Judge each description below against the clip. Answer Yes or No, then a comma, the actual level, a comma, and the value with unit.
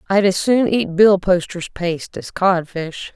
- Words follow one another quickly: No, average, 150 wpm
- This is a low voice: No, medium, 185 Hz